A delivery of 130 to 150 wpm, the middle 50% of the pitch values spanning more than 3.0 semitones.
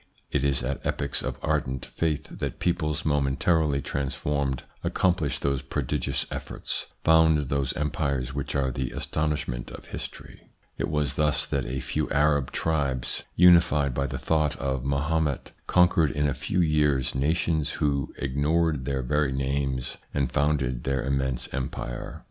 No: average, 145 wpm; narrow, 2.4 semitones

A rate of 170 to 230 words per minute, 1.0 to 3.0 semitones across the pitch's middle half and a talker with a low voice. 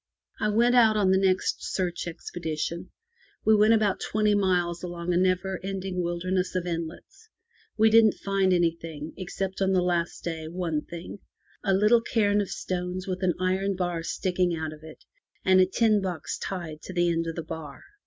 No: average, 185 wpm; narrow, 2.4 semitones; medium, 185 Hz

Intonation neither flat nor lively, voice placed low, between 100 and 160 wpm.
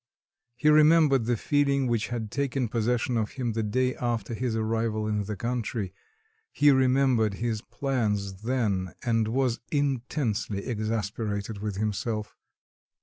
Yes: average, 3.2 semitones; low, 115 Hz; slow, 135 wpm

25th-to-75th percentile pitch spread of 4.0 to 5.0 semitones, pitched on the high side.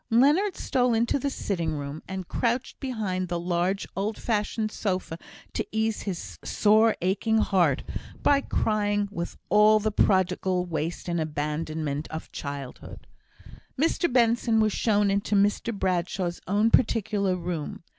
Yes: average, 4.3 semitones; high, 200 Hz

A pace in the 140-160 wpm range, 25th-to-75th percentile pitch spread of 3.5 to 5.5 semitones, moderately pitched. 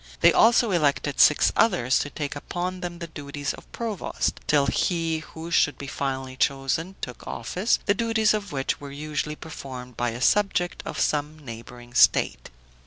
No: average, 170 wpm; average, 4.7 semitones; medium, 150 Hz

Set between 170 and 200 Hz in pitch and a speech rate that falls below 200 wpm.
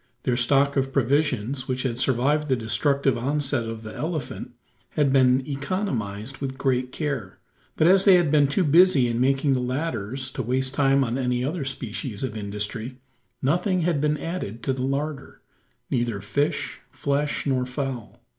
No: low, 135 Hz; average, 165 wpm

